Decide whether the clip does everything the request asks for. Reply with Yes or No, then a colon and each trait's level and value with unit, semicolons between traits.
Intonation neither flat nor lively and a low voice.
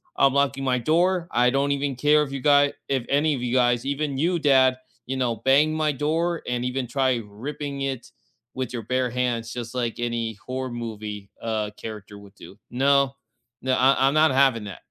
Yes: average, 3.0 semitones; low, 130 Hz